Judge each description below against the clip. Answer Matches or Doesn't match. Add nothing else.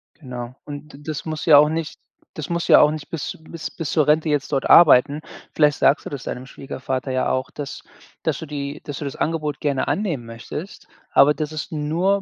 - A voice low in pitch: Doesn't match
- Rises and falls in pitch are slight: Matches